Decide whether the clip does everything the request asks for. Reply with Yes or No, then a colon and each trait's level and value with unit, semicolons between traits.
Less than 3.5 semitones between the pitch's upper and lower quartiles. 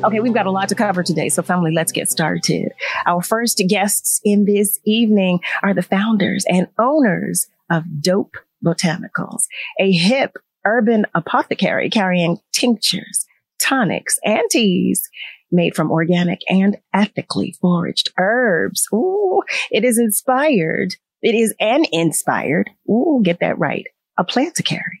No: average, 4.2 semitones